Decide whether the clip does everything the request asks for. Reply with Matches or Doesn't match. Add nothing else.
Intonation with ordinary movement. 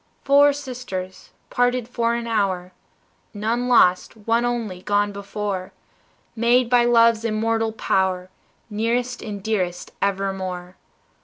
Matches